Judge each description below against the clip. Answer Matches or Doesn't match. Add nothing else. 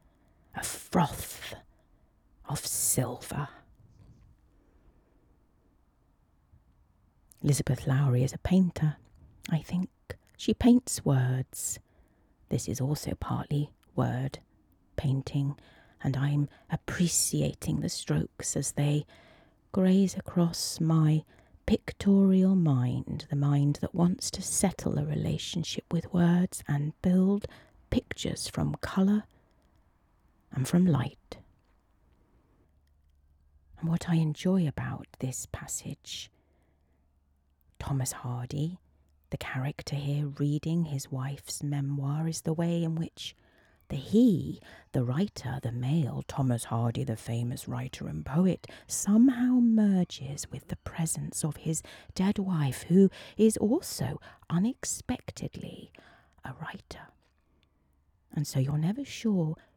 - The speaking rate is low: Matches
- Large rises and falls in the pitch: Matches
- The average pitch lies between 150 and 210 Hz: Doesn't match